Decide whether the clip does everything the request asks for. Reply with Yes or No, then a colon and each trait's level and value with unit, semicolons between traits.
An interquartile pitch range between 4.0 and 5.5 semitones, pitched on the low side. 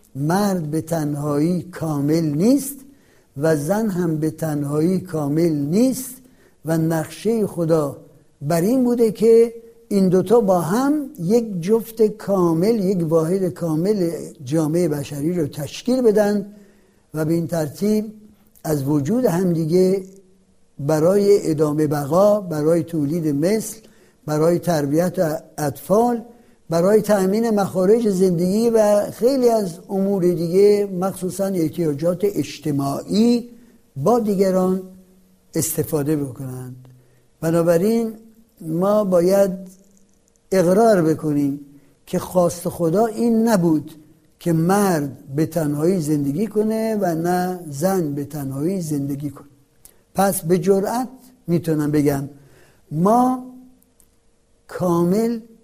No: average, 5.1 semitones; medium, 180 Hz